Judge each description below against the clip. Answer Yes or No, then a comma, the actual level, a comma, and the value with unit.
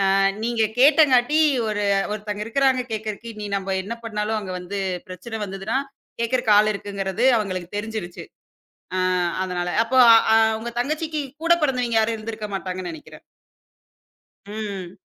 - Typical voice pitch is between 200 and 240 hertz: Yes, high, 215 Hz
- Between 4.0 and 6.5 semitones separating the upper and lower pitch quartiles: No, average, 3.4 semitones